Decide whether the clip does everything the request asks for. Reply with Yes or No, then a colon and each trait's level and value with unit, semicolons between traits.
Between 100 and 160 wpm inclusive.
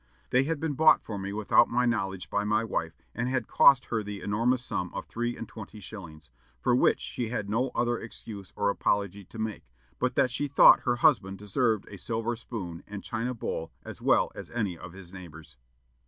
No: fast, 205 wpm